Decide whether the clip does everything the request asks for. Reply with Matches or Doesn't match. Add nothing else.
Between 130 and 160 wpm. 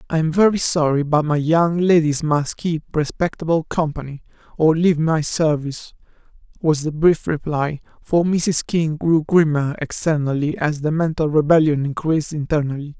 Matches